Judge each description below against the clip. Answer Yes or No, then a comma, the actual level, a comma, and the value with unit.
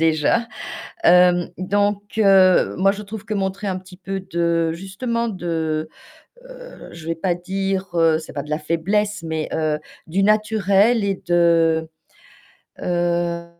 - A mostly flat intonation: No, average, 3.2 semitones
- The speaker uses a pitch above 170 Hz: Yes, medium, 185 Hz